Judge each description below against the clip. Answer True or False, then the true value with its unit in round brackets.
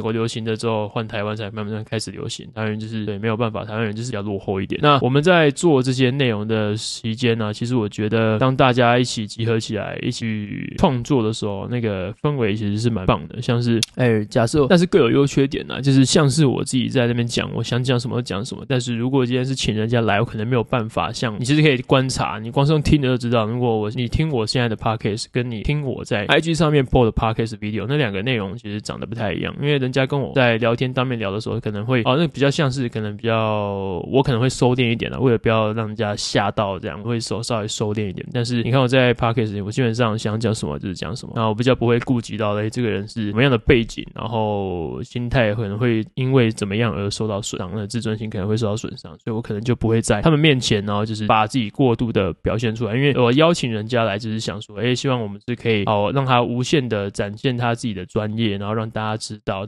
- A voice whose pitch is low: True (115 Hz)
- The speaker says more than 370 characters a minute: True (405 characters per minute)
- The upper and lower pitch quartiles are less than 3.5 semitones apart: True (2.8 semitones)